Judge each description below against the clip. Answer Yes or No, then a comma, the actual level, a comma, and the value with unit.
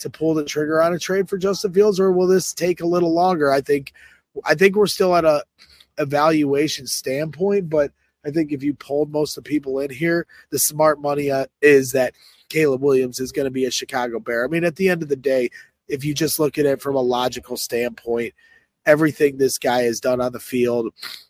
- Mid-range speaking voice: Yes, medium, 145 Hz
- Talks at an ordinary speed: No, fast, 225 wpm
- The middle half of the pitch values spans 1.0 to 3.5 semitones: No, average, 4.0 semitones